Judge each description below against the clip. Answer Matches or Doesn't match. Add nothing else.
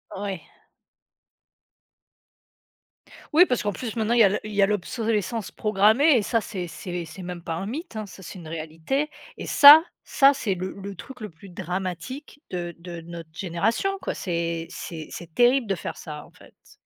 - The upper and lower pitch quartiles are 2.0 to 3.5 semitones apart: Doesn't match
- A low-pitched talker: Doesn't match